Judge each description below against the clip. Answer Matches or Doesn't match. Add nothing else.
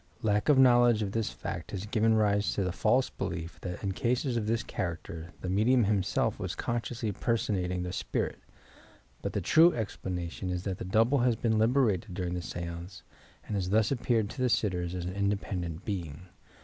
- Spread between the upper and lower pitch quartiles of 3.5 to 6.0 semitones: Matches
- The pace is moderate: Matches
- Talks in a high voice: Doesn't match